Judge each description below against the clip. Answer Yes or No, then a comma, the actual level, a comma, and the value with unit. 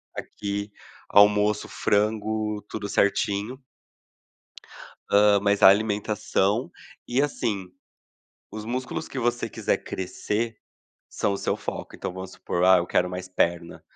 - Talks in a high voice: No, low, 105 Hz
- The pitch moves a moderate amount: No, narrow, 2.1 semitones